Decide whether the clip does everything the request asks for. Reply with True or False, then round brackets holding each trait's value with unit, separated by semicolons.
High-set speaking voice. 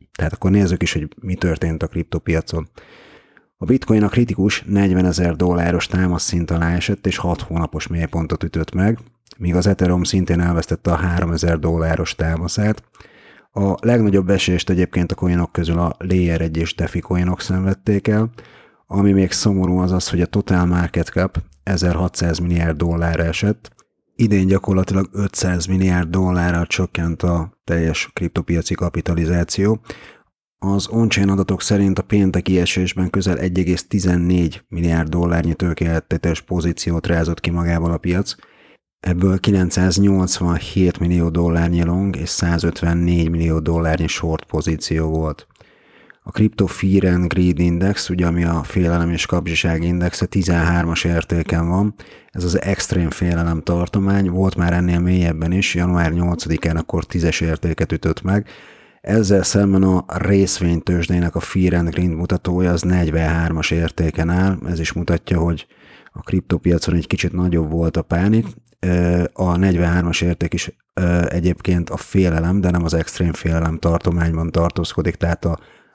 False (90 Hz)